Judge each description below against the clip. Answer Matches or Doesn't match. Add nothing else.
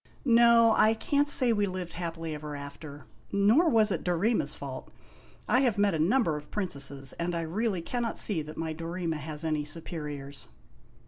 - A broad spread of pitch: Matches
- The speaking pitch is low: Doesn't match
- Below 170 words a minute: Doesn't match